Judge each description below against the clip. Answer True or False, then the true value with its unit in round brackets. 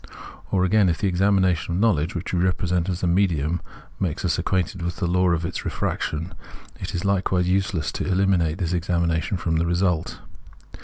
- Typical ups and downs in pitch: False (1.8 semitones)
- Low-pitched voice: True (90 Hz)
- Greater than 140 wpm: True (200 wpm)